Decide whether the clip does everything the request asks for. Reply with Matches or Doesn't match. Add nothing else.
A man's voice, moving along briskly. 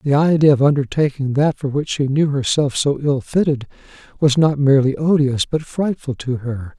Doesn't match